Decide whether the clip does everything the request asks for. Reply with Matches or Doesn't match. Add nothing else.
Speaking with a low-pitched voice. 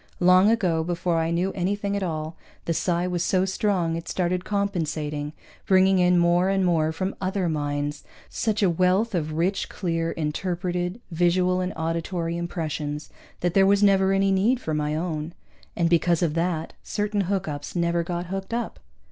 Doesn't match